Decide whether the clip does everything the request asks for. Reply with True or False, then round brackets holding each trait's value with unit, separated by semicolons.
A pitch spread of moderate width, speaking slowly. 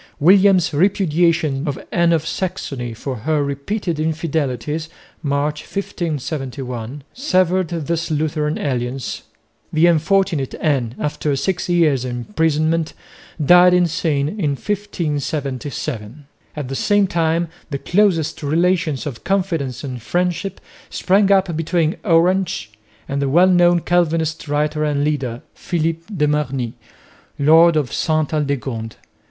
True (3.8 semitones; 115 wpm)